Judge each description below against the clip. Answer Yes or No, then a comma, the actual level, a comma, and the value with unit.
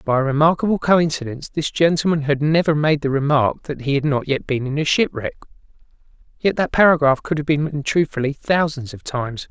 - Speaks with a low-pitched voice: No, medium, 150 Hz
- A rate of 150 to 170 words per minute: No, average, 195 wpm